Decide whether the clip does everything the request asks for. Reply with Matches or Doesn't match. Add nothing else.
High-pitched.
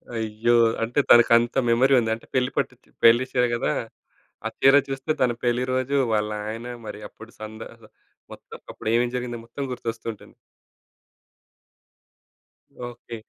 Doesn't match